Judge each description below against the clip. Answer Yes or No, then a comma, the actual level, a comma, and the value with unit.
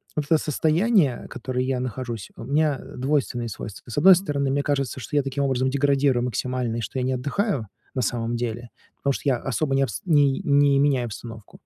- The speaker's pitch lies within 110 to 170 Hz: Yes, low, 135 Hz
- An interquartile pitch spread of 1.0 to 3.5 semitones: Yes, average, 2.8 semitones